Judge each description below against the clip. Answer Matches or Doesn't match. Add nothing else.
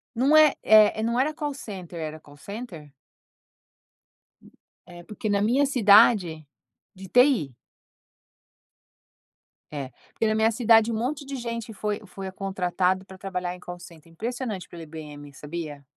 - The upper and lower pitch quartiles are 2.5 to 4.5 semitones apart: Doesn't match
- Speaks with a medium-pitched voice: Doesn't match